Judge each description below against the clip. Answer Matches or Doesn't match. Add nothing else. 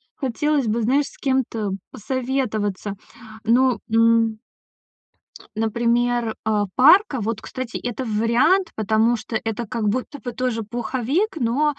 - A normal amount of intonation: Matches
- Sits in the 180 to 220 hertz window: Doesn't match